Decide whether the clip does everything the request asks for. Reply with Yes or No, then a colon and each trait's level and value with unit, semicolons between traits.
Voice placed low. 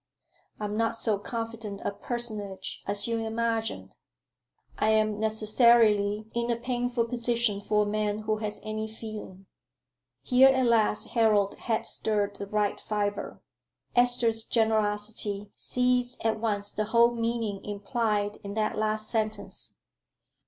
No: high, 215 Hz